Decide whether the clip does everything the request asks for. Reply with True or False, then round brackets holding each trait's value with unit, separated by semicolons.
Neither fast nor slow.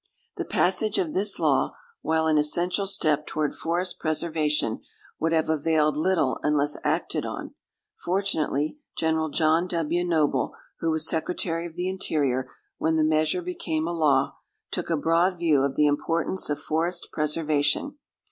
True (150 wpm)